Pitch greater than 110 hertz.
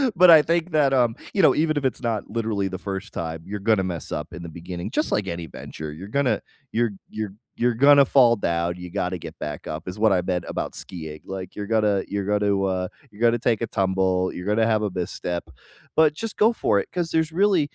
No: low, 105 Hz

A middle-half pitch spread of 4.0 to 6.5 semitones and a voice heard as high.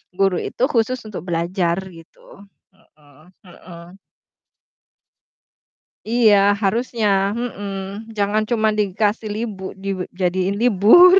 No: average, 3.3 semitones; high, 200 Hz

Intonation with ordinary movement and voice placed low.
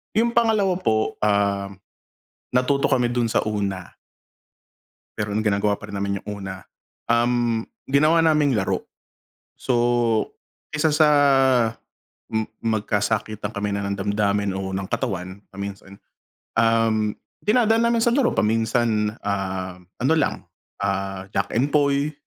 No: wide, 5.7 semitones; low, 110 Hz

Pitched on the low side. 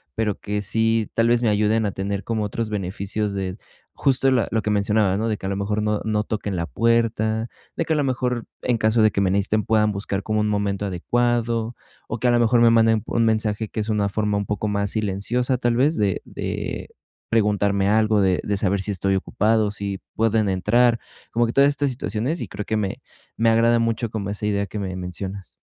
Yes: low, 110 Hz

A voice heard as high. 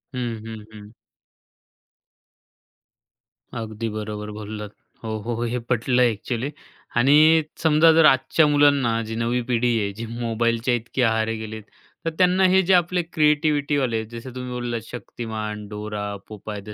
No: low, 115 Hz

